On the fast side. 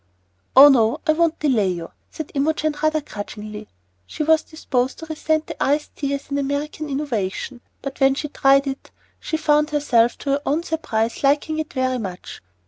No: average, 180 wpm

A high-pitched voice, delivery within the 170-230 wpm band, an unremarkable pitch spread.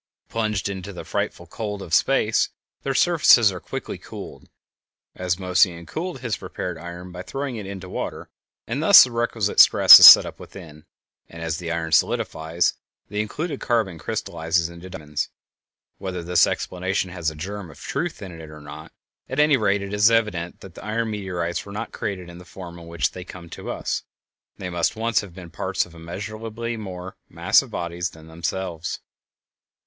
No: very low, 90 Hz; average, 180 wpm; average, 4.0 semitones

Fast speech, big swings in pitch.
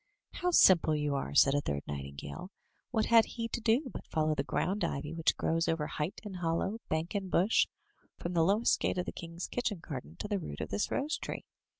Yes: fast, 225 wpm; wide, 5.7 semitones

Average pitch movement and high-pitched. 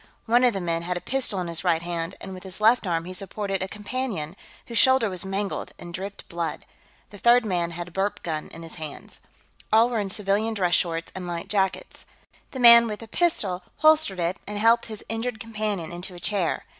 Yes: average, 4.4 semitones; high, 195 Hz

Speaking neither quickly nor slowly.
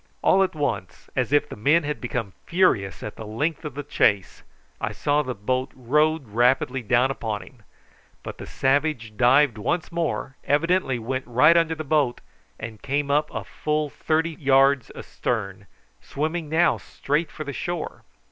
Yes: average, 165 wpm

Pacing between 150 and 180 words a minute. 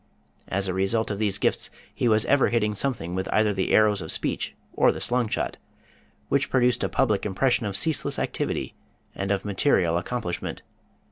Yes: average, 175 wpm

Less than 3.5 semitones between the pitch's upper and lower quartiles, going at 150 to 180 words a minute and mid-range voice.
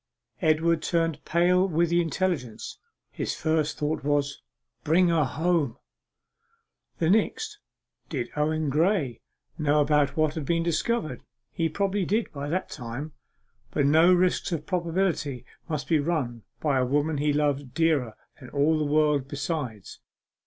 No: average, 2.9 semitones; average, 140 wpm; medium, 155 Hz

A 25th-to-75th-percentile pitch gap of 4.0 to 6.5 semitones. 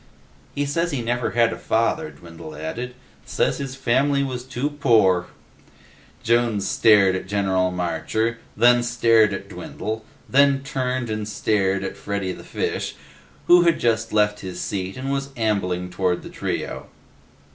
Yes: average, 5.0 semitones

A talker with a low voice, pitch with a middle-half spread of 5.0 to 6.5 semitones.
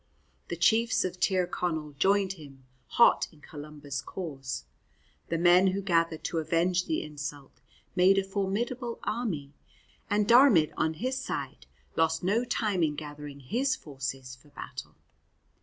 No: medium, 170 Hz; average, 5.3 semitones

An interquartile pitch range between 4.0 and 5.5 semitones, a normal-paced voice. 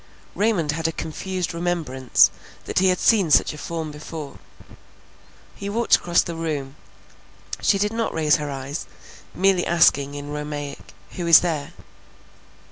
No: average, 3.5 semitones; average, 145 wpm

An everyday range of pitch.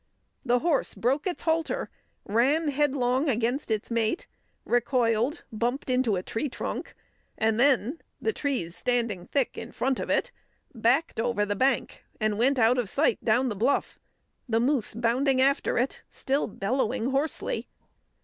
Yes: average, 3.4 semitones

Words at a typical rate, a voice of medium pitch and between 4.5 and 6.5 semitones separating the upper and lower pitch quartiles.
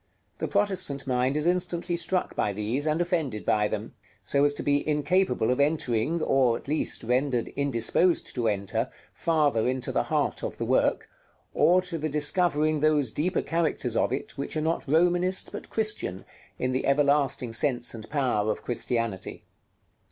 Yes: average, 165 wpm; medium, 145 Hz; average, 5.1 semitones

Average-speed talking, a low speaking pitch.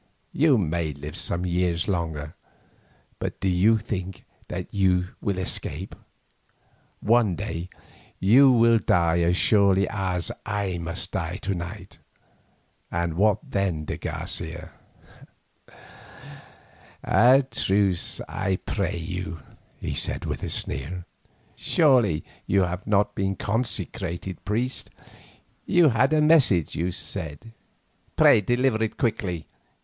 No: slow, 120 wpm; very low, 95 Hz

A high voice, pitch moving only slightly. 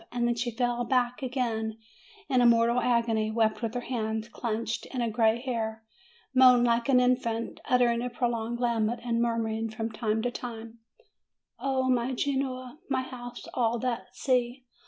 Yes: high, 240 Hz; narrow, 1.7 semitones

